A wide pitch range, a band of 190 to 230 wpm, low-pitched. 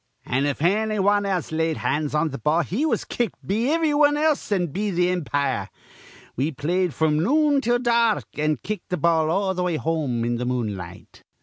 No: wide, 6.2 semitones; average, 195 wpm; medium, 175 Hz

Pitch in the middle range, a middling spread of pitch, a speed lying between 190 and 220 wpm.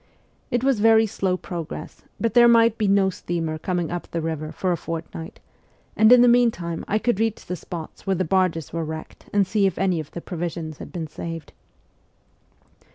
Yes: medium, 180 Hz; average, 4.7 semitones; average, 200 wpm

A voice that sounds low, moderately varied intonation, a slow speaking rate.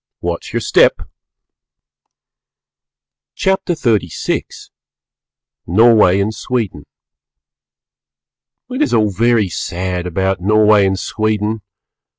Yes: low, 105 Hz; average, 3.2 semitones; slow, 85 wpm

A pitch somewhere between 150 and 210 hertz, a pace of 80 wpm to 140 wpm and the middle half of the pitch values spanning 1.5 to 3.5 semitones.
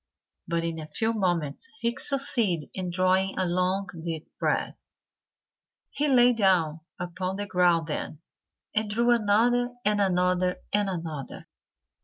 No: medium, 185 Hz; slow, 135 wpm; average, 4.1 semitones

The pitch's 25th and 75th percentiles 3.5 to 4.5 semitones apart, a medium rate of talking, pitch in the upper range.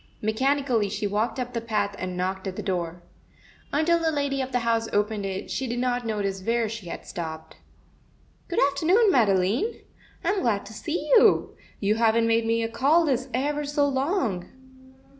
No: wide, 5.4 semitones; average, 180 wpm; high, 230 Hz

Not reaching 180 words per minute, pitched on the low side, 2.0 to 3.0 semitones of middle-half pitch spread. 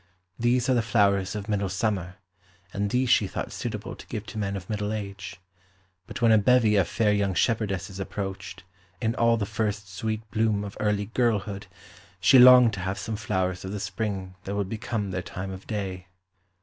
No: average, 190 wpm; low, 105 Hz; narrow, 2.4 semitones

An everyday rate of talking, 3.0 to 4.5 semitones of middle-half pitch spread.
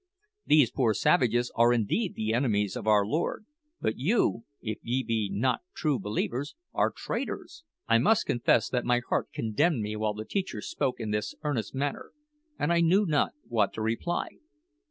No: average, 175 wpm; average, 5.1 semitones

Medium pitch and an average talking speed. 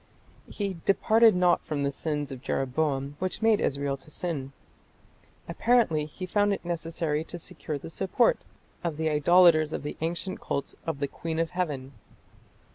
Yes: medium, 160 Hz; average, 160 wpm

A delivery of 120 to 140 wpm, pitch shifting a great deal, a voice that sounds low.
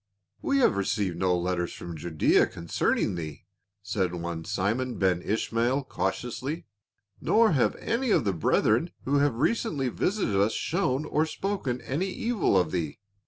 No: average, 160 wpm; wide, 8.3 semitones; low, 110 Hz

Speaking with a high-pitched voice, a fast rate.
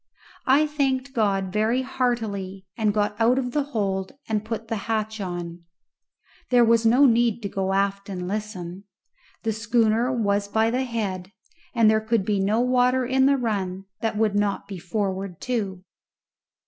No: high, 220 Hz; average, 165 wpm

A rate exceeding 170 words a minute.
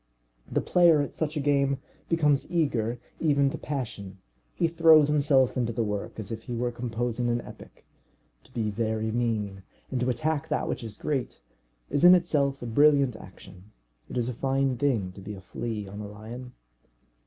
Yes: average, 185 wpm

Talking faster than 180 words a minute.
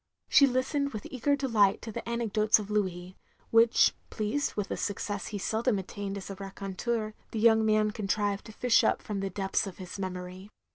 Yes: average, 190 wpm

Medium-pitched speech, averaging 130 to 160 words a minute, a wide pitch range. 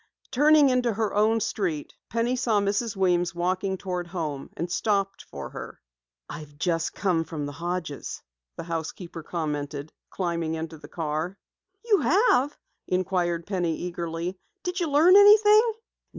Yes: medium, 180 Hz; average, 140 wpm; wide, 5.8 semitones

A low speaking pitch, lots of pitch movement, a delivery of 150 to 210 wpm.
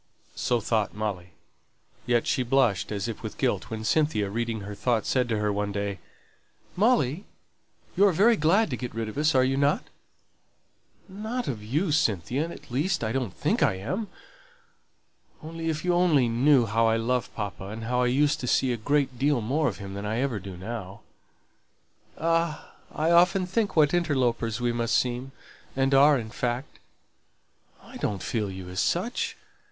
Yes: low, 125 Hz; wide, 6.0 semitones; average, 180 wpm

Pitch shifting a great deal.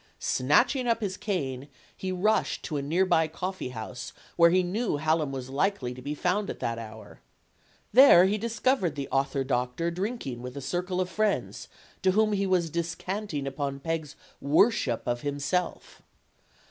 Yes: wide, 5.9 semitones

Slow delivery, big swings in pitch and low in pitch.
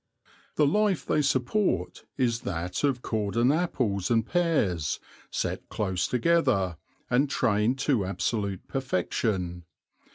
Yes: slow, 110 wpm; wide, 6.3 semitones; low, 115 Hz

